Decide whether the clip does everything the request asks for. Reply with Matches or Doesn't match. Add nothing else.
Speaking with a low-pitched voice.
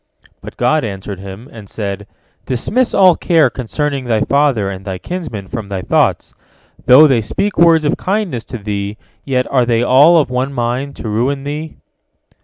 Matches